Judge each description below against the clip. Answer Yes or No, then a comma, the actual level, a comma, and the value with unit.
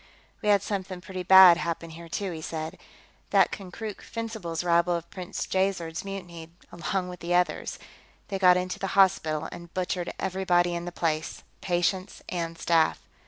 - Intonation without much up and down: Yes, narrow, 2.1 semitones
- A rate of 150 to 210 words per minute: Yes, average, 165 wpm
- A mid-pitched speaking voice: Yes, medium, 180 Hz